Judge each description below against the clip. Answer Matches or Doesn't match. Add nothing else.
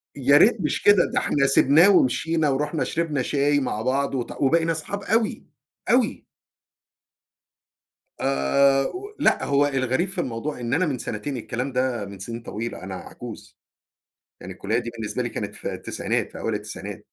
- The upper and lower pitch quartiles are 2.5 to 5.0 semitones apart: Doesn't match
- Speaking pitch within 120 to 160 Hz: Matches